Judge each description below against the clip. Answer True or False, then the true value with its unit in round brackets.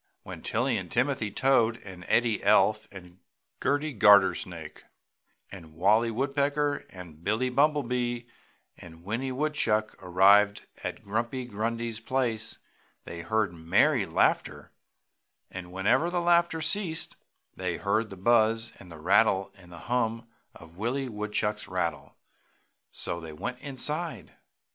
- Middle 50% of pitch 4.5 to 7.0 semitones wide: True (5.2 semitones)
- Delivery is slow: True (120 wpm)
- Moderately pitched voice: False (110 Hz)